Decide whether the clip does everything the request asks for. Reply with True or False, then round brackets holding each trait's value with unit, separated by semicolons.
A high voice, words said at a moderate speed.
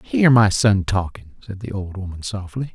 False (100 Hz; 195 wpm)